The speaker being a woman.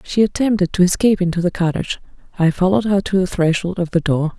Yes: female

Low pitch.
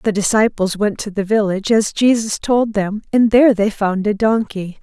No: high, 210 Hz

